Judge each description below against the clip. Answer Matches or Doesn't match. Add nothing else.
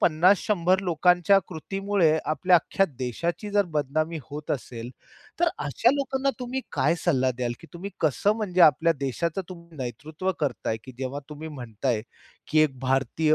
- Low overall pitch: Doesn't match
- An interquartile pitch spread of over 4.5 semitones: Matches